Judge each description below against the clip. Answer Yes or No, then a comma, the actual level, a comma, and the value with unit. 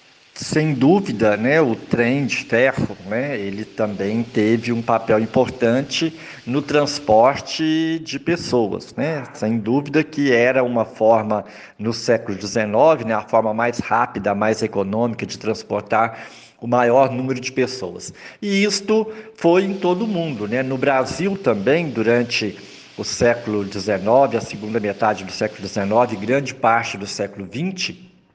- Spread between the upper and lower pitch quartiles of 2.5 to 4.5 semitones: No, average, 4.9 semitones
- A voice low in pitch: Yes, low, 120 Hz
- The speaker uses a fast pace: No, average, 145 wpm